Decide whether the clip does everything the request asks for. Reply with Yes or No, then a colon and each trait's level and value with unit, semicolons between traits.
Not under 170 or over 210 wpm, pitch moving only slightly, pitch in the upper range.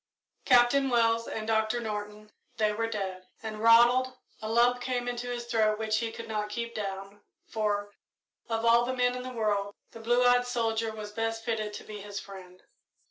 Yes: average, 190 wpm; narrow, 2.3 semitones; high, 225 Hz